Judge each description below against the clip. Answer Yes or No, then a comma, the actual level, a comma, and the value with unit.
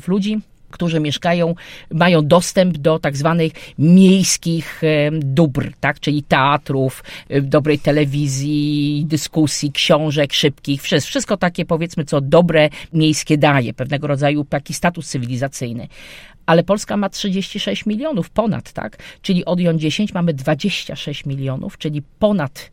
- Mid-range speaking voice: Yes, medium, 155 Hz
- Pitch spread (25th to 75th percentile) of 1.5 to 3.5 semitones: Yes, average, 3.2 semitones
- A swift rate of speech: No, average, 125 wpm